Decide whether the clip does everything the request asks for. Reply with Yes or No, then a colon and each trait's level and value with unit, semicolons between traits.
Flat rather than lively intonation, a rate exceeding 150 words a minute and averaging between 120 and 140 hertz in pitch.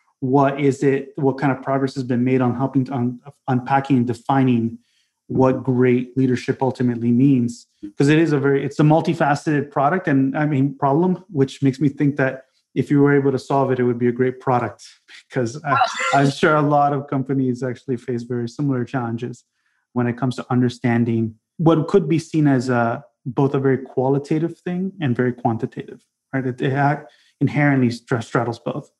Yes: narrow, 2.2 semitones; average, 190 wpm; low, 135 Hz